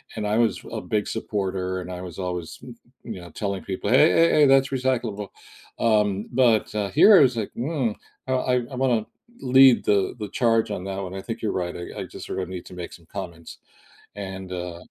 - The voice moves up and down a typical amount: Yes, average, 4.8 semitones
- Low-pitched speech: Yes, low, 105 Hz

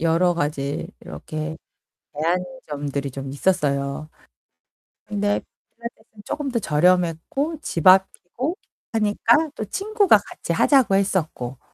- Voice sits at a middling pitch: Yes, medium, 180 Hz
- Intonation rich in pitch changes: Yes, wide, 7.3 semitones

